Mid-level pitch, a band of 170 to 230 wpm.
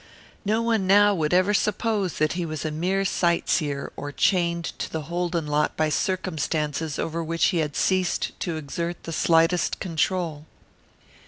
No: medium, 170 Hz; average, 160 wpm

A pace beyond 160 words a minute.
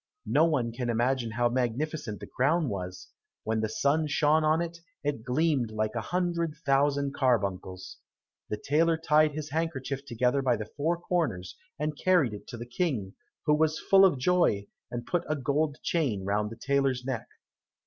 Yes: average, 175 wpm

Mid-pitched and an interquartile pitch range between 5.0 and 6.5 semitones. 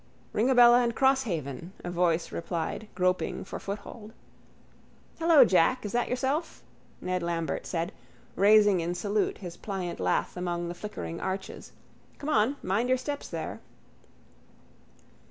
No: high, 195 Hz; wide, 5.6 semitones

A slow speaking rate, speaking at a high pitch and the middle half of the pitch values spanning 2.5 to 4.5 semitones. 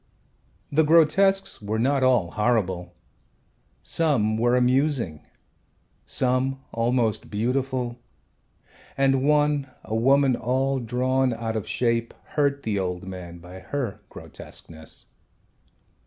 No: slow, 105 wpm; low, 125 Hz; average, 3.9 semitones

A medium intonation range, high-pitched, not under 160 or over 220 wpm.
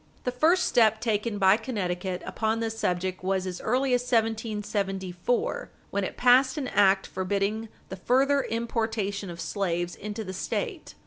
No: average, 3.8 semitones; high, 215 Hz; average, 150 wpm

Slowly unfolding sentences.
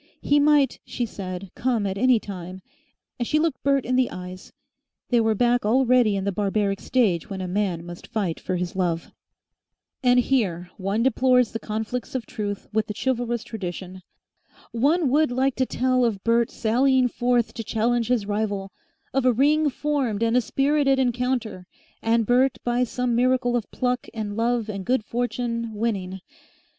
No: average, 170 wpm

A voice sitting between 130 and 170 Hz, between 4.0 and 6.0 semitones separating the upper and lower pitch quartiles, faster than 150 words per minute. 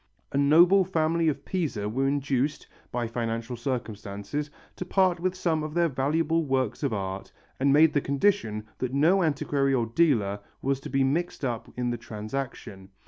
Yes: medium, 140 Hz; average, 5.2 semitones; average, 170 wpm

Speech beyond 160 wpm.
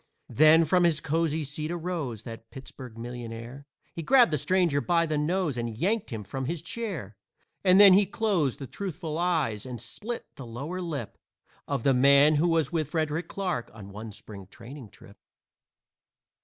Yes: average, 170 wpm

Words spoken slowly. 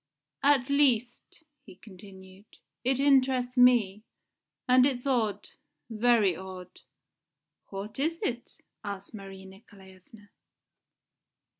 Yes: slow, 95 wpm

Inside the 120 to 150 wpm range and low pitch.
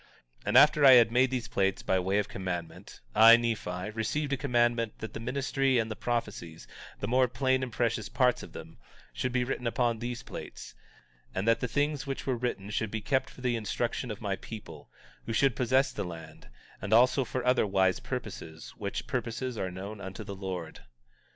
No: average, 200 wpm; low, 115 Hz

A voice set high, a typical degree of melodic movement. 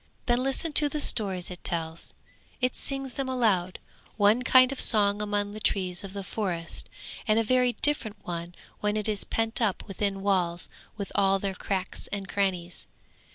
Yes: high, 205 Hz; average, 4.2 semitones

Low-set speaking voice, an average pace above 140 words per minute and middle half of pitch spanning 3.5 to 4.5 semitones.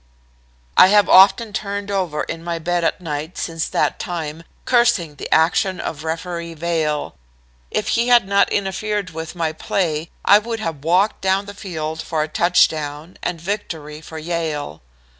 No: medium, 170 Hz; average, 160 wpm; average, 3.9 semitones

